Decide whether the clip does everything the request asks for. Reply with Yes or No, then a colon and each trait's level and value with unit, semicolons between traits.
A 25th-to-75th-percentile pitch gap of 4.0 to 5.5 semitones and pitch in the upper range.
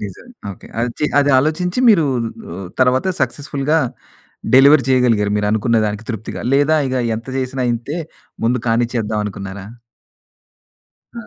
No: average, 4.6 semitones; low, 125 Hz